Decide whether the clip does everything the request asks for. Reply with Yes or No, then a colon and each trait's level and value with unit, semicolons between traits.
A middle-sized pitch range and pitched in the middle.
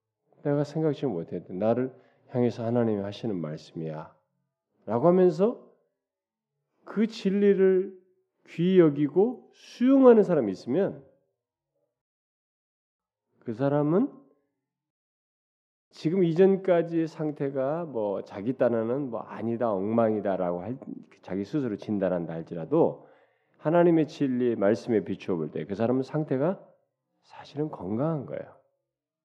No: wide, 7.9 semitones; medium, 145 Hz